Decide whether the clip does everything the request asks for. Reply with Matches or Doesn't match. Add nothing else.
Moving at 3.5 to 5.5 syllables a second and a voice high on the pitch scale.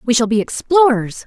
Matches